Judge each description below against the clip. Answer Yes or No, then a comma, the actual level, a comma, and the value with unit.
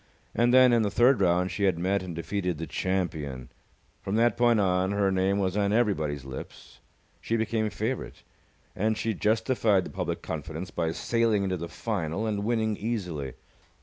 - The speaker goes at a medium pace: Yes, average, 175 wpm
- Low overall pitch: Yes, low, 100 Hz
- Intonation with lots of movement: No, average, 4.1 semitones